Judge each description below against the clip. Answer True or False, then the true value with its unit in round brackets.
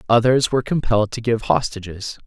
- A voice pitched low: True (115 Hz)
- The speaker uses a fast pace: False (160 wpm)